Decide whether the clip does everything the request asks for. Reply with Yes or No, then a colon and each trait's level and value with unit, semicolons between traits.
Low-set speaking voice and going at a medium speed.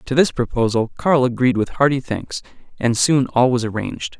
Yes: low, 125 Hz; average, 185 wpm